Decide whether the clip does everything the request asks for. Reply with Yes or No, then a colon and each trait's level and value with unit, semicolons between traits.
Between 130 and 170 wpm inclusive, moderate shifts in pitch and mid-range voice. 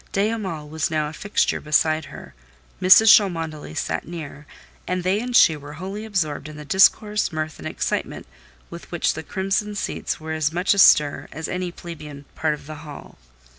No: average, 180 wpm; average, 3.9 semitones; medium, 160 Hz